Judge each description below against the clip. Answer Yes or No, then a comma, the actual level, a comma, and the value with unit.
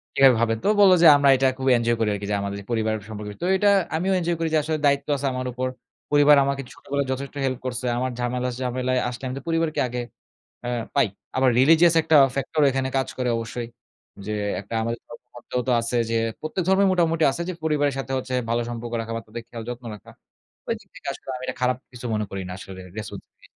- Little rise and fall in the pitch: No, average, 3.7 semitones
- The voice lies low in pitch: Yes, low, 130 Hz